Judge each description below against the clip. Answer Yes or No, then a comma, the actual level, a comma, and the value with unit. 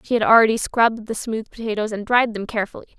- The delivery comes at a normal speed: No, fast, 220 wpm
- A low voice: No, high, 220 Hz